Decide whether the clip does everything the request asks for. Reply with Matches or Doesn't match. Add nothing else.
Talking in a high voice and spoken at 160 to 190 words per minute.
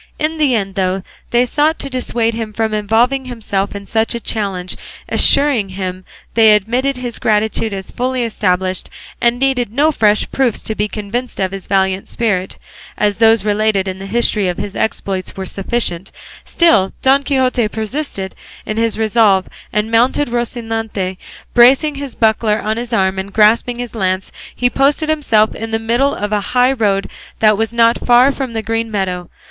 Matches